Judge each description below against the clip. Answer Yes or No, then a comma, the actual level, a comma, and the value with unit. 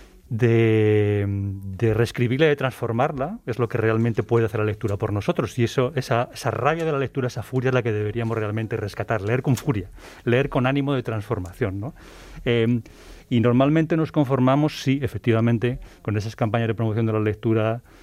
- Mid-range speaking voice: No, low, 115 Hz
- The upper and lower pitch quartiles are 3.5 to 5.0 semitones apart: No, average, 2.8 semitones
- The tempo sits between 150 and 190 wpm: Yes, average, 185 wpm